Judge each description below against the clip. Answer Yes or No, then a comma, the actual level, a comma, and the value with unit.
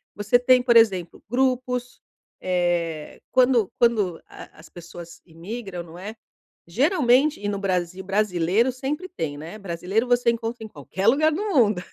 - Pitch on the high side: Yes, high, 210 Hz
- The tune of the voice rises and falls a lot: Yes, wide, 5.8 semitones